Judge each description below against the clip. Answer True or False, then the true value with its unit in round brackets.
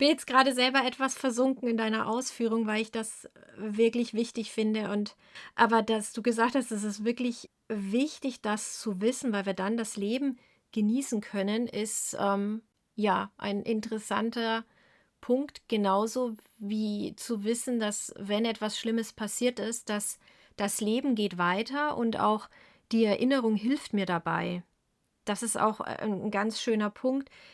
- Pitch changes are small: True (2.3 semitones)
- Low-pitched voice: False (225 Hz)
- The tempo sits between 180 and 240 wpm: False (155 wpm)